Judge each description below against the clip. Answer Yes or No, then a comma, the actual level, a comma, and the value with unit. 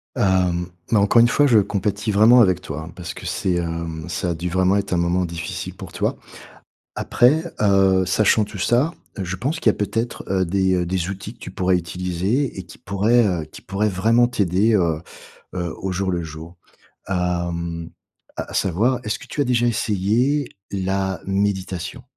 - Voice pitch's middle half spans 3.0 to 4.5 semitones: Yes, average, 3.5 semitones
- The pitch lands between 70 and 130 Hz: Yes, very low, 95 Hz